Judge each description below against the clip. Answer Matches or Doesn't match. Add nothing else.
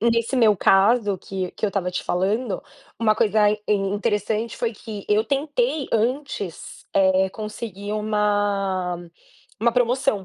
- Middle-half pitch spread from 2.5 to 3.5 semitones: Matches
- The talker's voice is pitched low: Doesn't match